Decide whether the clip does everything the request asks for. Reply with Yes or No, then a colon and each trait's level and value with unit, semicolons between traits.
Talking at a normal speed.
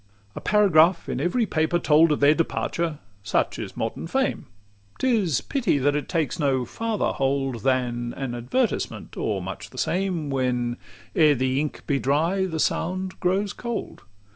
Yes: average, 165 wpm